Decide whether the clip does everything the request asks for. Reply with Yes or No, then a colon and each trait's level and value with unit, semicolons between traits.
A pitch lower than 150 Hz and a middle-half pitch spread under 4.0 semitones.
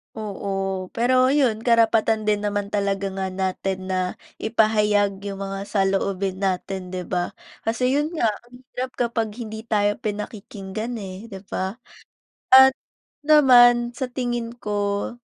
No: high, 210 Hz; average, 3.5 semitones